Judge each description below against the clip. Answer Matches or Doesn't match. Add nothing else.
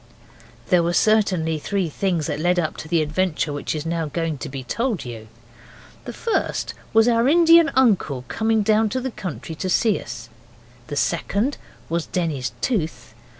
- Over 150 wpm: Matches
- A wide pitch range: Matches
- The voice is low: Doesn't match